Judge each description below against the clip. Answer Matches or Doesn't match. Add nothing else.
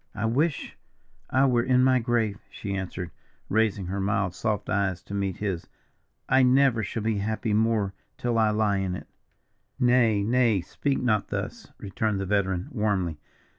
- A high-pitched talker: Doesn't match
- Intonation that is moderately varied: Matches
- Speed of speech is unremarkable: Matches